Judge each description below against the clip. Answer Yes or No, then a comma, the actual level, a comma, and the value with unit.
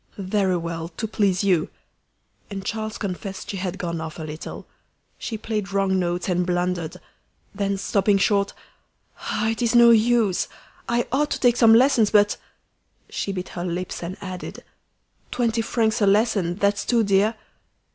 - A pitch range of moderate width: Yes, average, 3.4 semitones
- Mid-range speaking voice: No, high, 200 Hz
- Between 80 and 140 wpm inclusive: No, average, 165 wpm